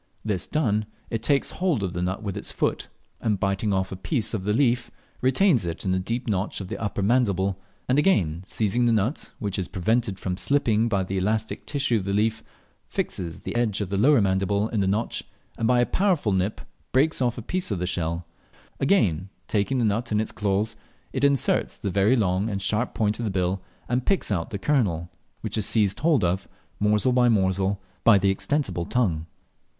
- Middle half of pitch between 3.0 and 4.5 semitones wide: Yes, average, 4.2 semitones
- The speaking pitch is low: Yes, low, 105 Hz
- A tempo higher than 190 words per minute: Yes, fast, 205 wpm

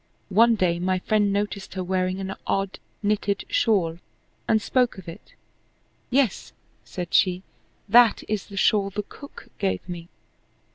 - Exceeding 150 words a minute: No, average, 145 wpm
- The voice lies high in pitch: Yes, high, 195 Hz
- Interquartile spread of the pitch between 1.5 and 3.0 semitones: Yes, narrow, 2.6 semitones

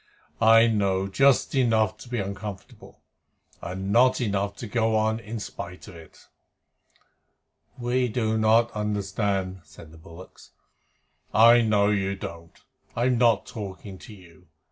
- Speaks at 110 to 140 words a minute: Yes, slow, 135 wpm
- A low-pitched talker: Yes, low, 105 Hz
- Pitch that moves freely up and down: No, average, 3.2 semitones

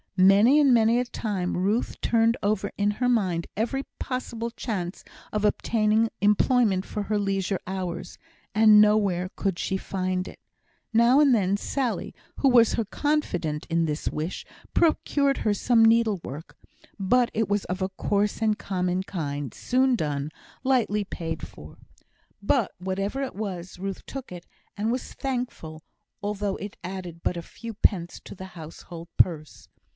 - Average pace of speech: Yes, average, 155 wpm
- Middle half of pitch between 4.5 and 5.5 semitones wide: No, average, 4.1 semitones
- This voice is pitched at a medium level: No, high, 205 Hz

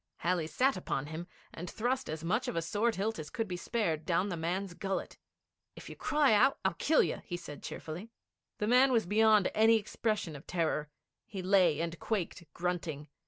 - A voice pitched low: No, medium, 185 Hz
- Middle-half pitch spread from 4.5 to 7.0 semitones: Yes, average, 5.0 semitones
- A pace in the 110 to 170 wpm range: No, average, 195 wpm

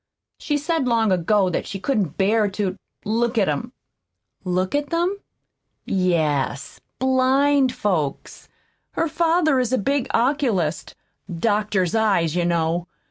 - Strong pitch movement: Yes, wide, 6.7 semitones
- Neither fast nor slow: No, slow, 130 wpm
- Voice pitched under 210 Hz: No, high, 215 Hz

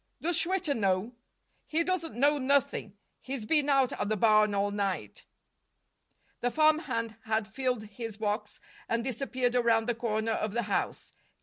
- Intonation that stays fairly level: No, average, 4.4 semitones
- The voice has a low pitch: No, high, 230 Hz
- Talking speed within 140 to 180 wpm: Yes, average, 150 wpm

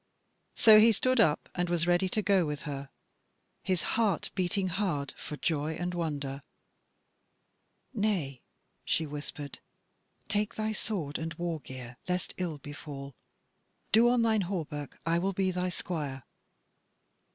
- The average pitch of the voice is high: No, medium, 175 Hz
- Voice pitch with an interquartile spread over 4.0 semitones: Yes, average, 5.0 semitones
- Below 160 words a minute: Yes, average, 140 wpm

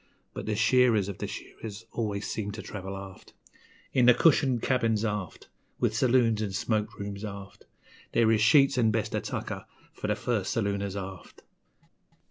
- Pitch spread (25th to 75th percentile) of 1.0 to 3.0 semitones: Yes, narrow, 2.6 semitones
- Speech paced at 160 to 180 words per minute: Yes, average, 165 wpm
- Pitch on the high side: No, low, 110 Hz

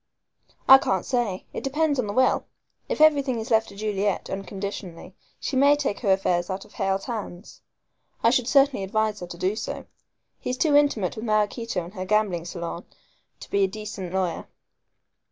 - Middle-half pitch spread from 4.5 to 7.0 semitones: Yes, average, 4.8 semitones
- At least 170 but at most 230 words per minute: Yes, average, 180 wpm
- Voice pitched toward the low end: No, high, 210 Hz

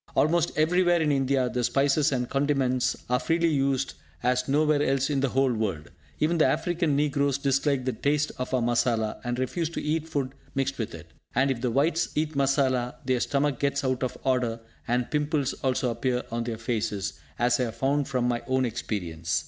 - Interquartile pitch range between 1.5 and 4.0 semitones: Yes, average, 2.9 semitones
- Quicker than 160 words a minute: Yes, average, 195 wpm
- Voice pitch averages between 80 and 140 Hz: Yes, low, 135 Hz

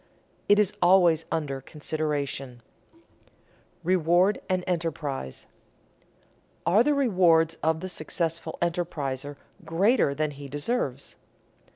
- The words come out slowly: Yes, slow, 100 wpm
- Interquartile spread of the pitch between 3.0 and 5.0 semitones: Yes, average, 4.1 semitones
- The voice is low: No, medium, 165 Hz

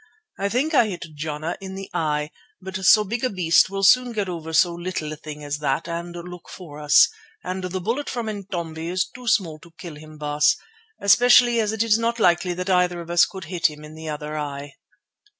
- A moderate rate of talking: No, fast, 220 wpm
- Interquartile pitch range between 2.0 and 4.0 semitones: No, average, 4.4 semitones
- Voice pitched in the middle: Yes, medium, 175 Hz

